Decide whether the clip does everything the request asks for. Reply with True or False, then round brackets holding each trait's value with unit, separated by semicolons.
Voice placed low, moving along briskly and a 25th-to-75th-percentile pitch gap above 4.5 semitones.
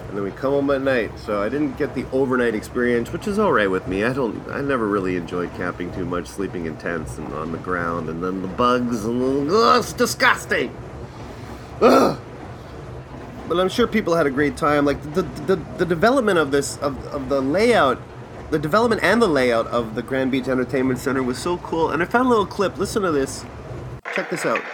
True (130 Hz; 220 wpm; 5.6 semitones)